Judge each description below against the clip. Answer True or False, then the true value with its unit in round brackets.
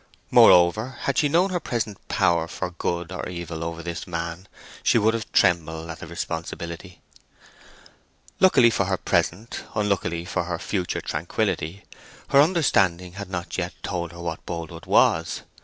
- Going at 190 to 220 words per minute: False (155 wpm)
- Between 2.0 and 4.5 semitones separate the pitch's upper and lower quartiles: True (3.6 semitones)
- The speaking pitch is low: True (90 Hz)